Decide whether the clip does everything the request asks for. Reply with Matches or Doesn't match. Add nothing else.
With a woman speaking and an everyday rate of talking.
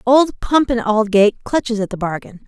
Matches